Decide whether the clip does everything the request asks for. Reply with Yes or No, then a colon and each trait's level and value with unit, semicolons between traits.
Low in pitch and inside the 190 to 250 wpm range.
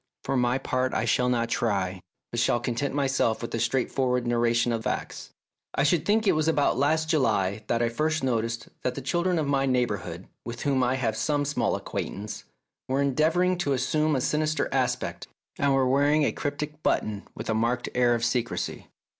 Yes: low, 130 Hz; average, 195 wpm